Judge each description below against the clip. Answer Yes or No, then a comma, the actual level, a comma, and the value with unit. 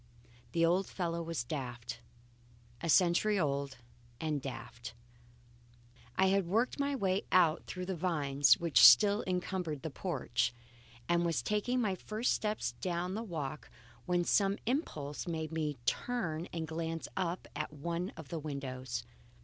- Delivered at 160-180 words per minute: No, average, 145 wpm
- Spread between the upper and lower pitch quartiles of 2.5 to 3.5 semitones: No, average, 4.4 semitones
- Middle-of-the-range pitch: Yes, medium, 170 Hz